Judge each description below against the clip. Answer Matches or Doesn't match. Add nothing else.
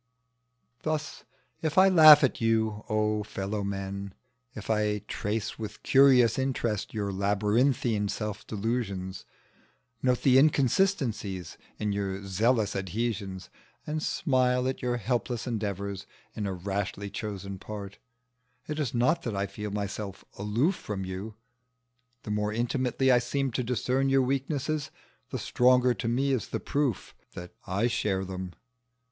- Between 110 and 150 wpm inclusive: Matches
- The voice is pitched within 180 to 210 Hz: Doesn't match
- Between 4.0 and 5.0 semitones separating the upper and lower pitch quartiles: Matches